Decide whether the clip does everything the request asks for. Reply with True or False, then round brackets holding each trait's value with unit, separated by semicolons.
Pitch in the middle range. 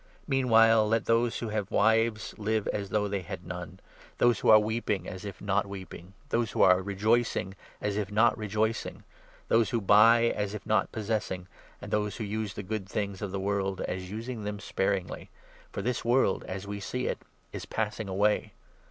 False (105 Hz)